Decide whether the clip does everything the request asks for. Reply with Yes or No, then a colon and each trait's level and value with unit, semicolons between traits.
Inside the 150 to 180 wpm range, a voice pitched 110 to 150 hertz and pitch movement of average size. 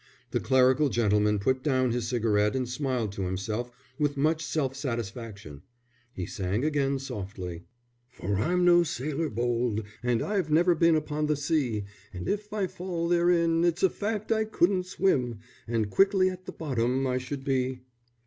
No: average, 165 wpm; low, 135 Hz; wide, 6.4 semitones